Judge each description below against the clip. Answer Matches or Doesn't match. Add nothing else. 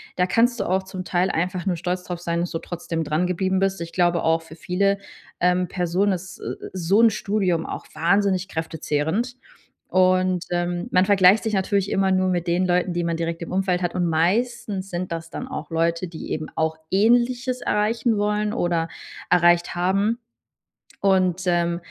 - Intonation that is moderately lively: Doesn't match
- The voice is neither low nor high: Matches